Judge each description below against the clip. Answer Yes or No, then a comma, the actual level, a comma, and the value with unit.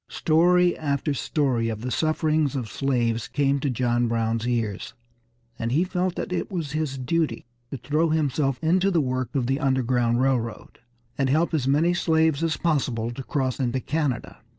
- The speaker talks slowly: No, average, 175 wpm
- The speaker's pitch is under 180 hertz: Yes, low, 135 Hz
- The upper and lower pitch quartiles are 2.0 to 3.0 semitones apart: No, average, 4.4 semitones